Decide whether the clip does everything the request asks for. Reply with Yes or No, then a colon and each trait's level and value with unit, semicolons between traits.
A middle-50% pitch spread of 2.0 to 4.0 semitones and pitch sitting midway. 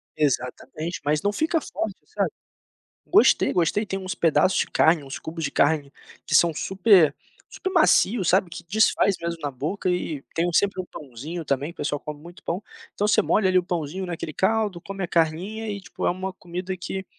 Yes: average, 3.6 semitones; medium, 175 Hz